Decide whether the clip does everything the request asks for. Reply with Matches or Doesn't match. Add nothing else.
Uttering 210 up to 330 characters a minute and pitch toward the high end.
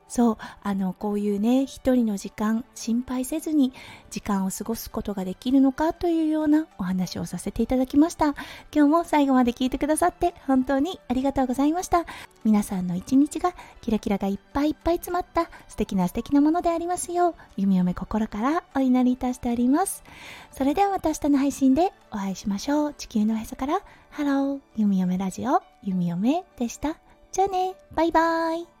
Doesn't match